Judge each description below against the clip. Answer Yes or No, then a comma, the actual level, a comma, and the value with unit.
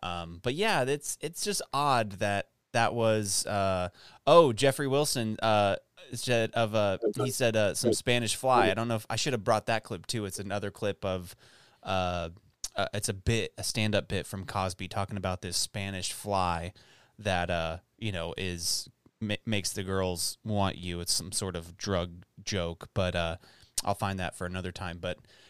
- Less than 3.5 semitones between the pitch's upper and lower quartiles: No, average, 3.8 semitones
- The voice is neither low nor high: No, low, 100 Hz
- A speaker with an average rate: Yes, average, 190 wpm